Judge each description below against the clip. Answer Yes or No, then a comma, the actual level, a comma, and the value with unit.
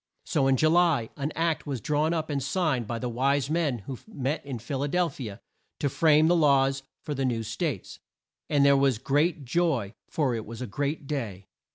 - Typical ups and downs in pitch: Yes, average, 3.8 semitones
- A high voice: No, medium, 140 Hz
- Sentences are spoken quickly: Yes, fast, 215 wpm